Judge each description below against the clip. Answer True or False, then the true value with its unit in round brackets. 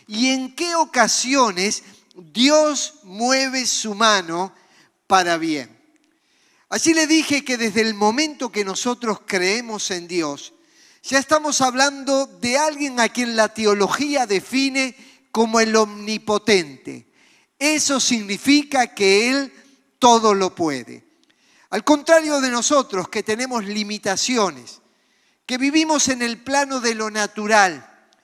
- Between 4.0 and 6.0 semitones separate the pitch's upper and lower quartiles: True (5.1 semitones)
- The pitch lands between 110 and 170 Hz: False (240 Hz)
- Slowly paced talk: True (120 wpm)